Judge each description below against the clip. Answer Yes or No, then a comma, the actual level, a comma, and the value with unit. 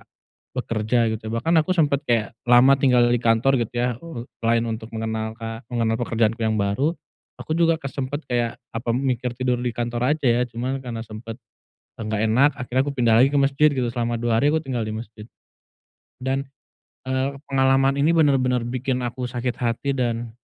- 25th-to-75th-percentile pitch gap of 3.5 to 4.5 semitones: No, average, 2.8 semitones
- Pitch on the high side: No, low, 120 Hz